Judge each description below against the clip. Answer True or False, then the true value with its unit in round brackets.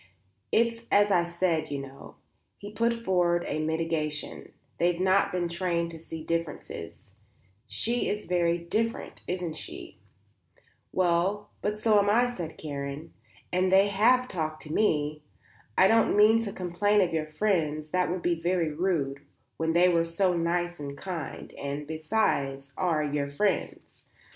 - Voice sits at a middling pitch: True (170 Hz)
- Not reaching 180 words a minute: True (150 wpm)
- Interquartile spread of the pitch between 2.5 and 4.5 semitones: True (3.7 semitones)